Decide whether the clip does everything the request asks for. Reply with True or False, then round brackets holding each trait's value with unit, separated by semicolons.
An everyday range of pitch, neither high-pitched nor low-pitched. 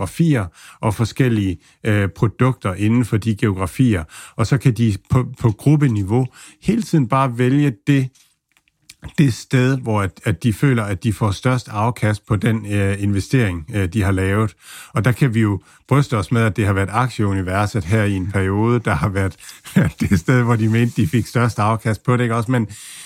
False (3.6 semitones; 115 Hz)